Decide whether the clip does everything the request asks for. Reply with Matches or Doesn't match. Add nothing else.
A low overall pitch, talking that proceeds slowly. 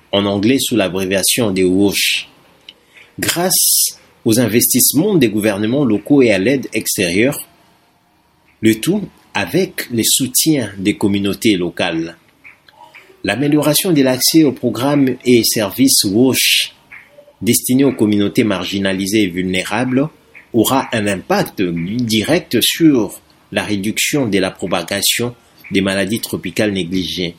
Matches